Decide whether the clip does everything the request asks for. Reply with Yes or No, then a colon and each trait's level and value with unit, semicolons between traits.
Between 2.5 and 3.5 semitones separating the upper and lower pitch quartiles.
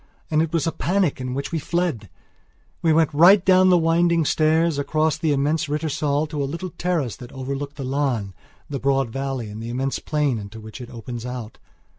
No: average, 4.1 semitones